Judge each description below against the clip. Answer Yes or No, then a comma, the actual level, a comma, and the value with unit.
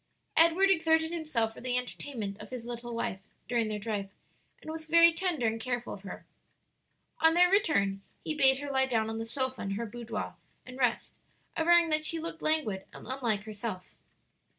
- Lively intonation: Yes, wide, 6.3 semitones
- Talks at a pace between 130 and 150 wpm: No, average, 185 wpm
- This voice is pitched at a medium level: No, very high, 255 Hz